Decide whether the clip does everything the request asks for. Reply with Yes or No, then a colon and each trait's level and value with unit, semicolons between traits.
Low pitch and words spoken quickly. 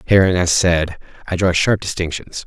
No: very low, 90 Hz; average, 170 wpm